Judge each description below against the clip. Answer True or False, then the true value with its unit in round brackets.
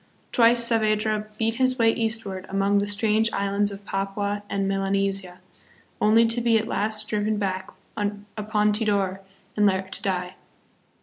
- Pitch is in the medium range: False (205 Hz)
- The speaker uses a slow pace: False (145 wpm)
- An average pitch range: False (1.9 semitones)